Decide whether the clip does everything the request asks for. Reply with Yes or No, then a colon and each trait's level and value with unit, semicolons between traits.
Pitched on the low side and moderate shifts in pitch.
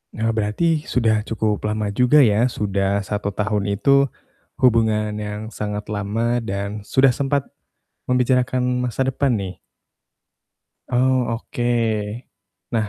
Yes: low, 110 Hz; average, 3.4 semitones